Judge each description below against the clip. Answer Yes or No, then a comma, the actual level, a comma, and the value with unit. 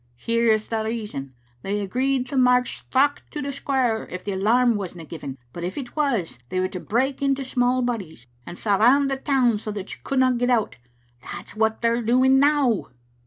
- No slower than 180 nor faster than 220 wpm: Yes, average, 190 wpm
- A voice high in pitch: Yes, high, 235 Hz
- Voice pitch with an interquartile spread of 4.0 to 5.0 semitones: Yes, average, 4.5 semitones